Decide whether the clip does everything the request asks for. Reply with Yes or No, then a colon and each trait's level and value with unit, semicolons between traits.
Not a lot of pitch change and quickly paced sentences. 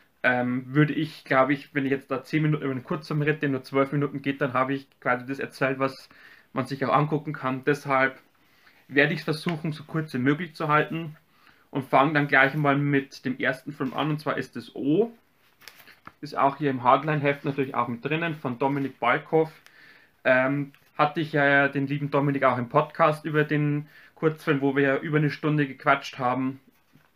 Yes: narrow, 2.1 semitones; fast, 200 wpm